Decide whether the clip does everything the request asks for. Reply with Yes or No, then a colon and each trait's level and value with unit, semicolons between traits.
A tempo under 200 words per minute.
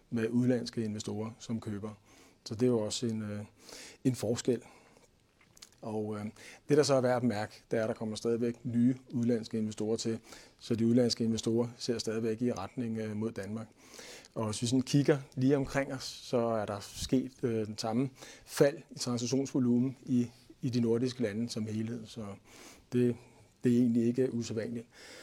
Yes: average, 180 wpm